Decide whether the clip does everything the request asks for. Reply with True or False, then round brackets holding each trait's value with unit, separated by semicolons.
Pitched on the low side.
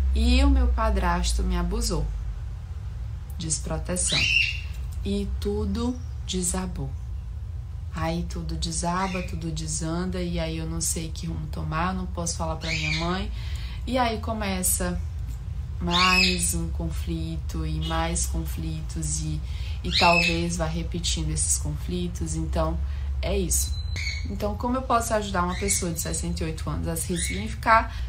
True (80 Hz)